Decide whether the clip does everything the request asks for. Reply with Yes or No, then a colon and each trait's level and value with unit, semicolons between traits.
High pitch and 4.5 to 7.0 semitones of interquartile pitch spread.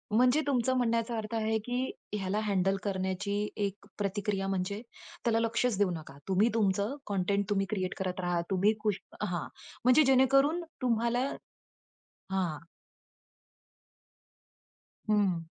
No: high, 205 Hz; average, 3.6 semitones